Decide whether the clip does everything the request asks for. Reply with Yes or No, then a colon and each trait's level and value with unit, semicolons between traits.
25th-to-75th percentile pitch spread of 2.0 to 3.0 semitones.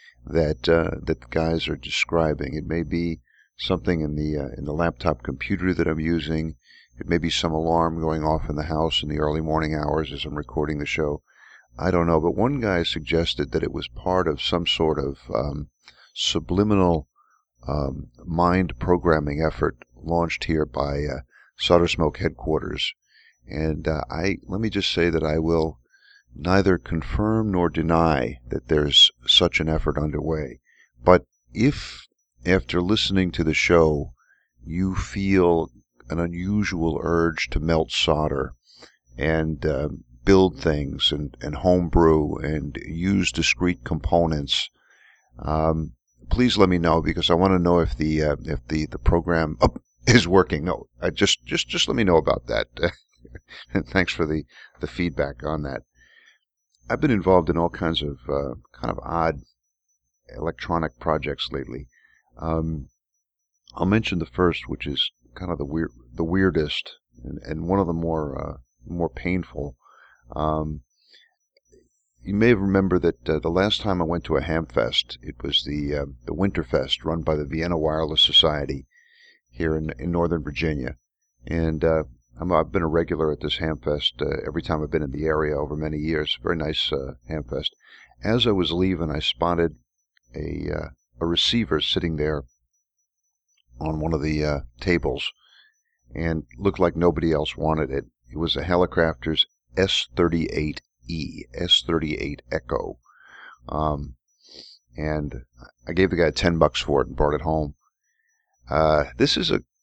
Yes: narrow, 2.5 semitones